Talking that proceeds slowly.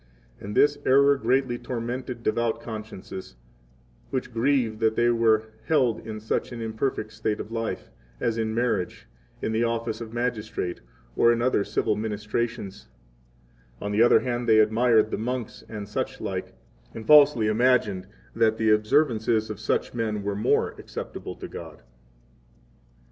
No: average, 150 wpm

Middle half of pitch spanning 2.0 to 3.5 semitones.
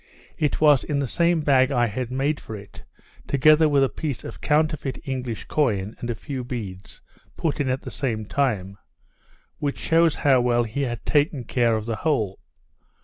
No: average, 4.0 semitones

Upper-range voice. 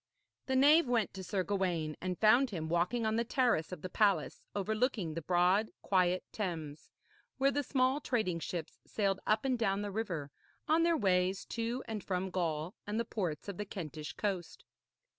Yes: high, 195 Hz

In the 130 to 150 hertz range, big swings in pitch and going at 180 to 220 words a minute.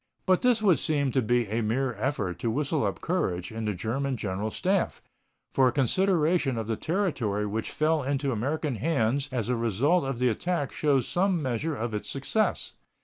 Yes: low, 135 Hz; wide, 5.8 semitones; average, 190 wpm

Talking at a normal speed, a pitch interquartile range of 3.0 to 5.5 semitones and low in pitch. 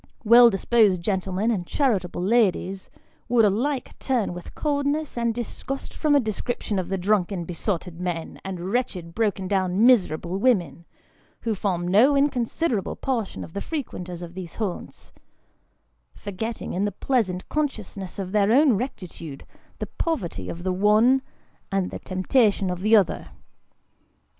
No: average, 145 wpm; average, 4.8 semitones; high, 200 Hz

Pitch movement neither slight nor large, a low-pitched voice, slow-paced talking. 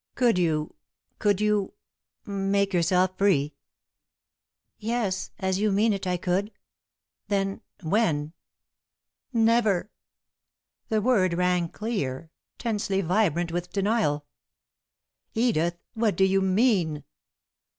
No: average, 3.4 semitones; high, 195 Hz; slow, 100 wpm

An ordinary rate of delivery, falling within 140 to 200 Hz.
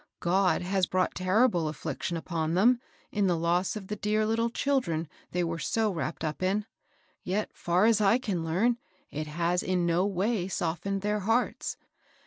Yes: average, 170 wpm; medium, 185 Hz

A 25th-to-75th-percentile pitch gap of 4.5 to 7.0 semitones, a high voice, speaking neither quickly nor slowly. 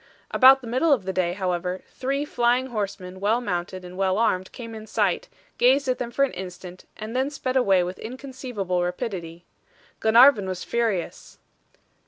Yes: wide, 5.6 semitones; high, 215 Hz; average, 170 wpm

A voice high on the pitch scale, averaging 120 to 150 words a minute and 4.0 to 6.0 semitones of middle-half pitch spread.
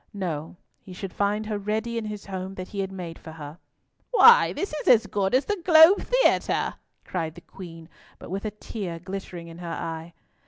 No: high, 195 Hz; average, 200 wpm; average, 4.3 semitones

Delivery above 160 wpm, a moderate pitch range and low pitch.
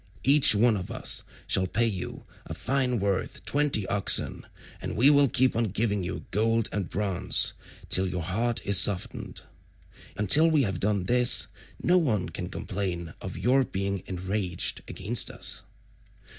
No: average, 155 wpm; average, 4.6 semitones; low, 105 Hz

